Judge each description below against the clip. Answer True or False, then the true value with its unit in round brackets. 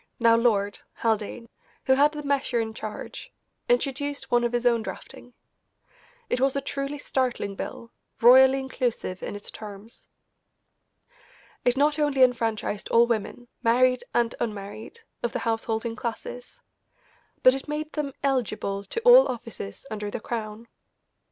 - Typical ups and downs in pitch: True (3.4 semitones)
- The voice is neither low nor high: False (240 Hz)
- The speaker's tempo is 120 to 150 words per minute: True (140 wpm)